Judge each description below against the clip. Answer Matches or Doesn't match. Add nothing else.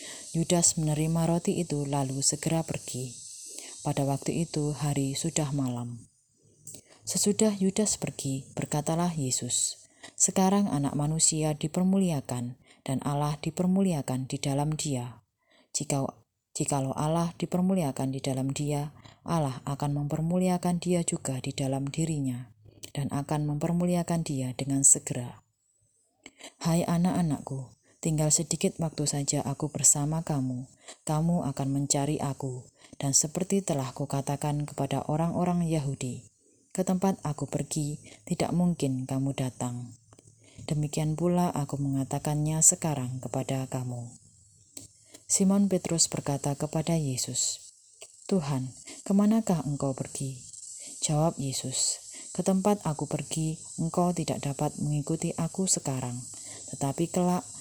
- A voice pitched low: Doesn't match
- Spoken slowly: Doesn't match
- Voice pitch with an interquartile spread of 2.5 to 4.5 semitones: Matches